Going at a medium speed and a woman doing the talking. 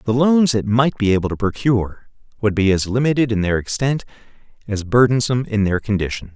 No: average, 190 wpm; male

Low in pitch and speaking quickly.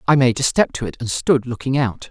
Yes: low, 125 Hz; fast, 285 wpm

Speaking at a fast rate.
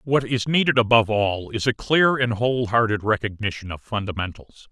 No: average, 165 wpm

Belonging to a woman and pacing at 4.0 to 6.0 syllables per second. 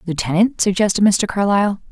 No: female; 6.2 syllables/s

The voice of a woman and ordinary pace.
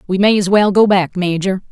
No: female; fast, 245 wpm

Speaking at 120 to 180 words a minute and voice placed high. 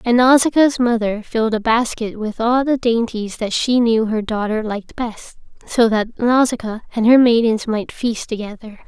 Yes: average, 175 wpm; high, 230 Hz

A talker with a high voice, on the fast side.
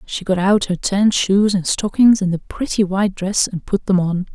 Yes: high, 195 Hz; fast, 235 wpm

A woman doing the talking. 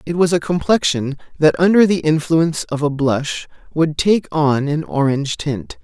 No: male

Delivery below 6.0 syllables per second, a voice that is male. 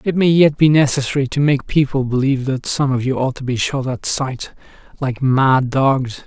Yes: 4.9 syllables/s; male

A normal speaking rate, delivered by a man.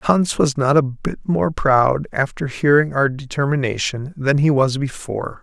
Yes: average, 165 wpm; male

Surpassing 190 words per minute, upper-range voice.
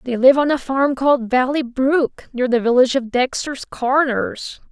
No: average, 180 wpm; very high, 260 Hz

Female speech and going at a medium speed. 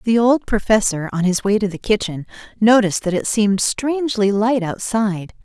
Yes: female; average, 175 wpm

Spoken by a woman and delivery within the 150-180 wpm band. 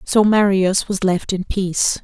Yes: female; average, 175 wpm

